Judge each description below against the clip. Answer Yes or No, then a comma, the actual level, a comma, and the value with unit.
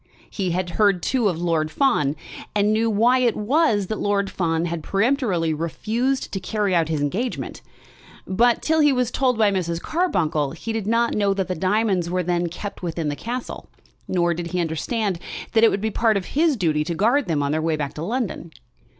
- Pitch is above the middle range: Yes, high, 195 Hz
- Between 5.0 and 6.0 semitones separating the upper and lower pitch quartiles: Yes, average, 5.3 semitones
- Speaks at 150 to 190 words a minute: No, fast, 205 wpm